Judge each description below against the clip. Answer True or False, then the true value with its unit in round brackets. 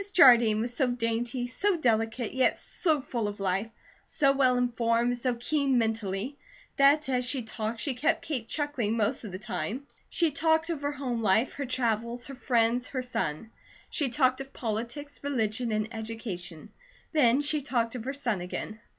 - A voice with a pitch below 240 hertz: False (245 Hz)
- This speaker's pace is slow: False (175 wpm)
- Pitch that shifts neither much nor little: True (3.6 semitones)